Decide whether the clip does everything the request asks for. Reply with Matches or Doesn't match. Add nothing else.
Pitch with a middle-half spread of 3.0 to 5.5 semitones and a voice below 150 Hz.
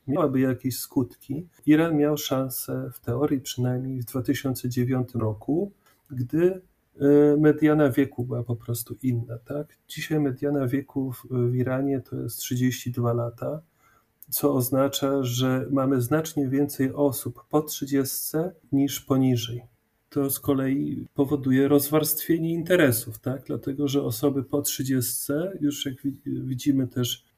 Doesn't match